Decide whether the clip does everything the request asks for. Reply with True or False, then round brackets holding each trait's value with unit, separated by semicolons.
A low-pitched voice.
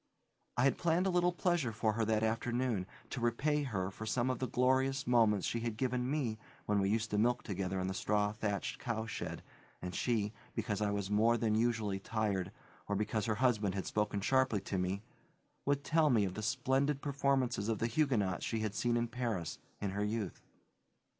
True (110 Hz)